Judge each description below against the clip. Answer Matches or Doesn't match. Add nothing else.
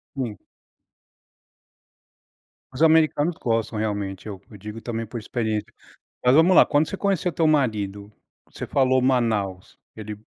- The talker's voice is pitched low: Matches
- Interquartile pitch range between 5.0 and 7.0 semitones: Matches